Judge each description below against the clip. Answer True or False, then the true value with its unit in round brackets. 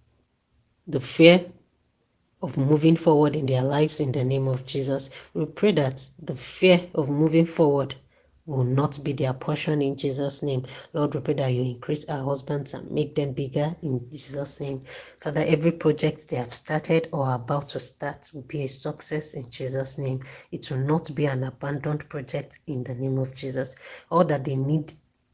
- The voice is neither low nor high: True (145 Hz)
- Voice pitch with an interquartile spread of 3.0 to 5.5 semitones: False (2.5 semitones)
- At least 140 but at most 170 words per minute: False (185 wpm)